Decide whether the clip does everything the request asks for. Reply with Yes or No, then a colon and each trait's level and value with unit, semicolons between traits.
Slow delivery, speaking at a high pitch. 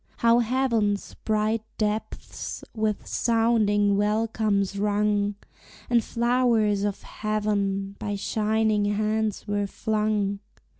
Yes: slow, 95 wpm; high, 210 Hz